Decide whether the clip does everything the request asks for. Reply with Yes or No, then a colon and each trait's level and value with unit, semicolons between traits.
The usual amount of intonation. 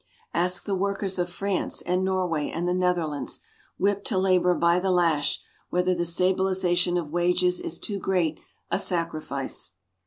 No: narrow, 1.6 semitones